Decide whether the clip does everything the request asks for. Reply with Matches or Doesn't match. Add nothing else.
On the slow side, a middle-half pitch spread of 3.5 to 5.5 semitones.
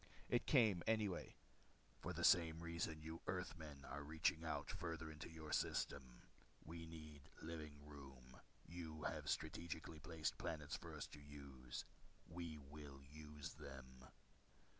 Doesn't match